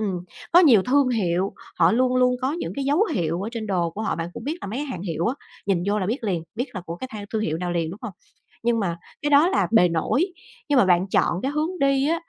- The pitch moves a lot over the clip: Yes, wide, 7.3 semitones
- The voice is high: Yes, high, 220 Hz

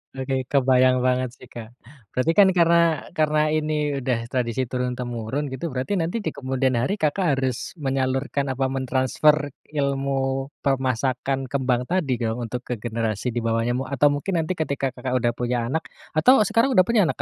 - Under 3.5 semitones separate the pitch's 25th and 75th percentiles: Yes, average, 2.9 semitones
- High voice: No, low, 130 Hz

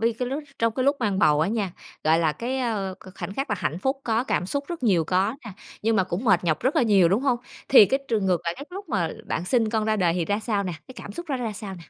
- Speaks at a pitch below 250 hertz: Yes, high, 215 Hz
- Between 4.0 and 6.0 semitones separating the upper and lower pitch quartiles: Yes, average, 5.1 semitones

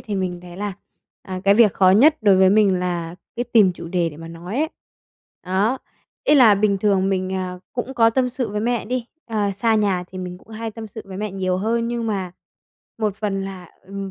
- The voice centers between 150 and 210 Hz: Yes, high, 200 Hz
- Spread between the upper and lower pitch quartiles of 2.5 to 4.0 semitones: Yes, average, 3.3 semitones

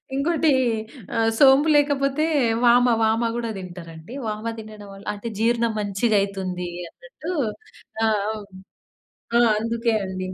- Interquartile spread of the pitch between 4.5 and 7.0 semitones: Yes, average, 4.9 semitones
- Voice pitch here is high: Yes, high, 225 Hz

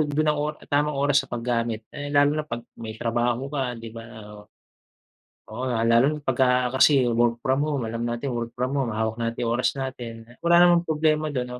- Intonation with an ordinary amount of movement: Yes, average, 3.6 semitones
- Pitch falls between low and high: No, low, 125 Hz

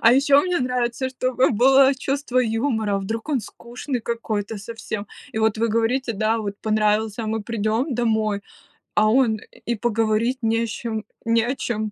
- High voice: Yes, high, 230 Hz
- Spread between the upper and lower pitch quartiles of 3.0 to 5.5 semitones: No, narrow, 2.6 semitones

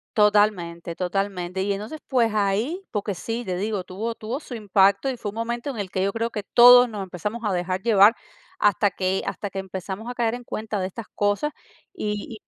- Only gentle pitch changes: No, average, 3.1 semitones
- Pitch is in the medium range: No, high, 205 Hz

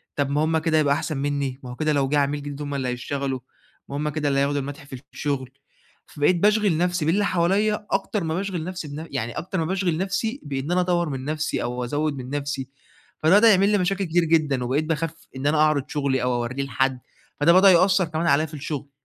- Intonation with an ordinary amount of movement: Yes, average, 4.0 semitones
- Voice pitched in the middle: Yes, medium, 150 Hz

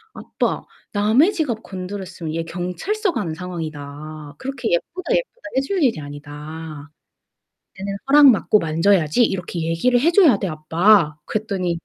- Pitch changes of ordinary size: No, wide, 7.4 semitones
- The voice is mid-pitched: Yes, medium, 180 Hz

